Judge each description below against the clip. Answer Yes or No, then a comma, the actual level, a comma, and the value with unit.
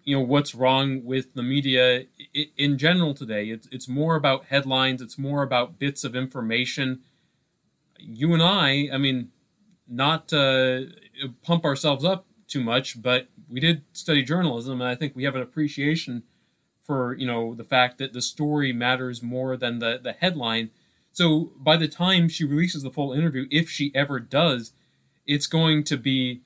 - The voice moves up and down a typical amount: Yes, average, 3.2 semitones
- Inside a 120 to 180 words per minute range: Yes, average, 175 wpm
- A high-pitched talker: No, low, 135 Hz